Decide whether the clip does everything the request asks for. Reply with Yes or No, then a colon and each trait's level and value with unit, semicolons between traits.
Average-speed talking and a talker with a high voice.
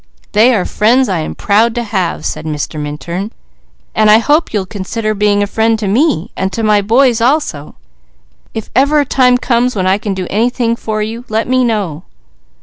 Yes: average, 190 wpm; high, 215 Hz